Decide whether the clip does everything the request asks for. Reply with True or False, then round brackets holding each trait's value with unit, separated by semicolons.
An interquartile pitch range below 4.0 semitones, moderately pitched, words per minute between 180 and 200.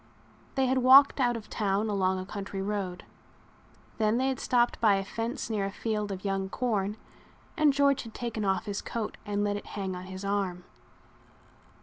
False (3.5 semitones; 210 Hz; 190 wpm)